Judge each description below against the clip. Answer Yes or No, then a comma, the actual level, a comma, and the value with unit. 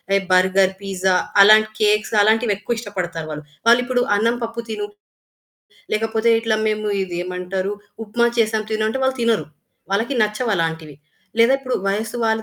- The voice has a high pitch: Yes, high, 215 Hz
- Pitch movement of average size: Yes, average, 3.1 semitones